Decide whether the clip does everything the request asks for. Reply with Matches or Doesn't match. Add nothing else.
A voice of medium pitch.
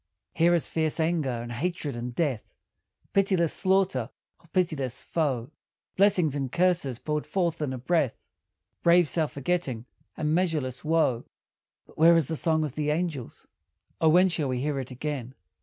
Matches